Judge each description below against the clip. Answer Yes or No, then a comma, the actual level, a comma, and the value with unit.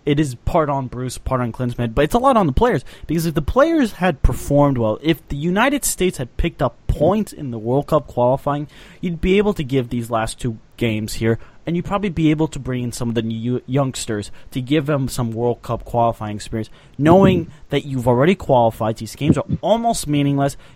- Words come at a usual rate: No, fast, 220 wpm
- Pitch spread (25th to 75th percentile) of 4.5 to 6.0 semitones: Yes, wide, 5.6 semitones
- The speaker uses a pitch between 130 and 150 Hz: Yes, low, 135 Hz